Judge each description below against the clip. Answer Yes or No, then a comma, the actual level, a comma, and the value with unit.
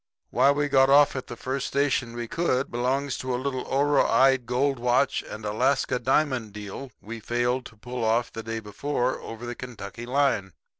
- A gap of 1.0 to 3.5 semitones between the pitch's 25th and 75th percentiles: Yes, narrow, 2.6 semitones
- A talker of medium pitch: No, low, 125 Hz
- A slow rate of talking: No, average, 185 wpm